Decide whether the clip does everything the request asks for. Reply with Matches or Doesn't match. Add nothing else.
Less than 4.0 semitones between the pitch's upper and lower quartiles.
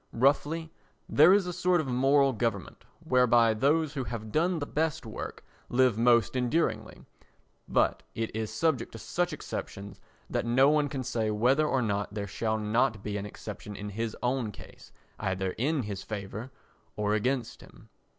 Doesn't match